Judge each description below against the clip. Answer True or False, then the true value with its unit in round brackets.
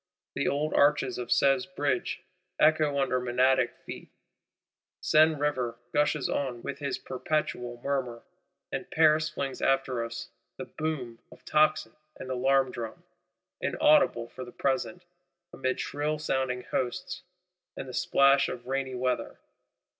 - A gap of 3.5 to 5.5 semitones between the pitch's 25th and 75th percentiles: False (2.8 semitones)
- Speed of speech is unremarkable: False (130 wpm)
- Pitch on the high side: False (135 Hz)